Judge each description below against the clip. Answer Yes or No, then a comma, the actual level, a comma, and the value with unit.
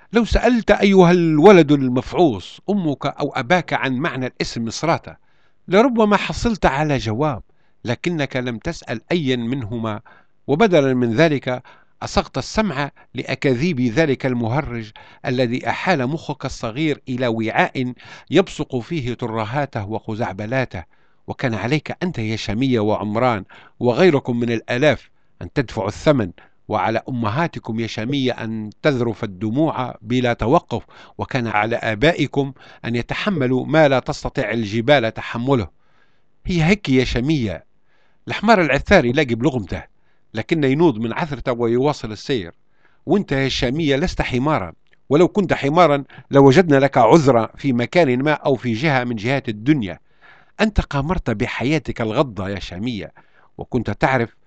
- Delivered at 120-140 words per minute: Yes, average, 125 wpm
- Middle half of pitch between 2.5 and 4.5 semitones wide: No, average, 5.0 semitones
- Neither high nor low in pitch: No, low, 130 Hz